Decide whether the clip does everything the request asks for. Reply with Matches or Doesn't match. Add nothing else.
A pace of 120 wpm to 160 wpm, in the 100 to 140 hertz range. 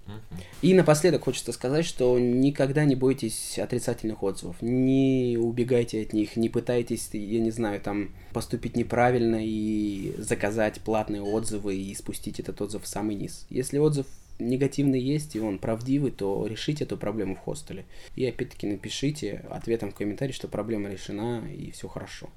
Matches